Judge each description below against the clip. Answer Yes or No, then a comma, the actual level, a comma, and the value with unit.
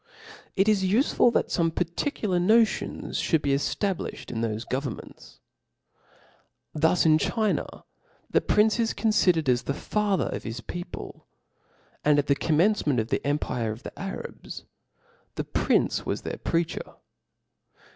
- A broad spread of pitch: Yes, wide, 6.9 semitones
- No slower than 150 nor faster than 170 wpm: No, average, 140 wpm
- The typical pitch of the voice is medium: Yes, medium, 170 Hz